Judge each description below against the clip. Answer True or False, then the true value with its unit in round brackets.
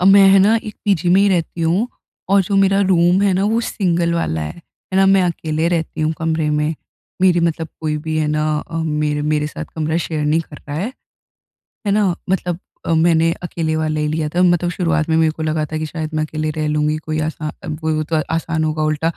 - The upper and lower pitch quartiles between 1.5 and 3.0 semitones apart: True (2.4 semitones)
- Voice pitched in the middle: True (160 Hz)